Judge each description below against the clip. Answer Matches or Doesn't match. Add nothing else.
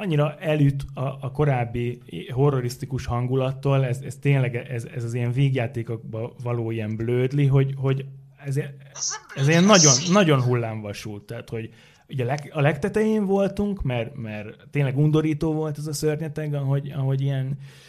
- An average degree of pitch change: Matches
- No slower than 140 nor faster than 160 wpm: Matches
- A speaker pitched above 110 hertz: Matches